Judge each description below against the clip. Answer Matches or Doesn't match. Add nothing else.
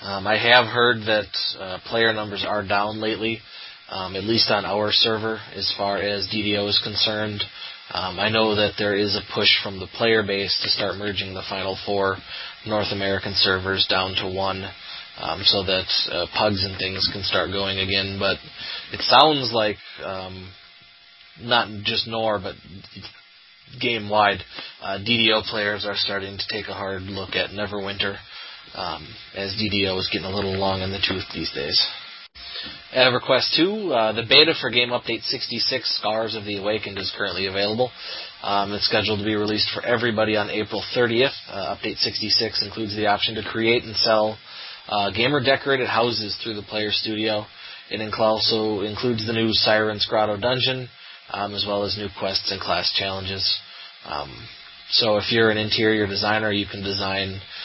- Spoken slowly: Doesn't match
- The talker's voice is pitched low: Matches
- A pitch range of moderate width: Doesn't match